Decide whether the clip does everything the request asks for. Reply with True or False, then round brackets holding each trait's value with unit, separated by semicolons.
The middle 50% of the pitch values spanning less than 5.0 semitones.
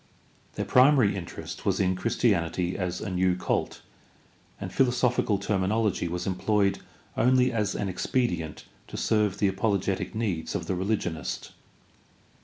True (3.5 semitones)